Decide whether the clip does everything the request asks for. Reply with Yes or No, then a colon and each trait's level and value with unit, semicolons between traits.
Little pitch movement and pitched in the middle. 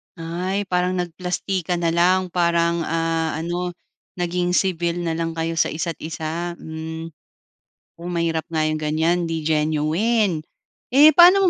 Yes: narrow, 1.7 semitones; medium, 170 Hz